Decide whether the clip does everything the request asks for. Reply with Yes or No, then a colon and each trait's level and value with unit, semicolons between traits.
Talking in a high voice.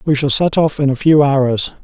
No: medium, 140 Hz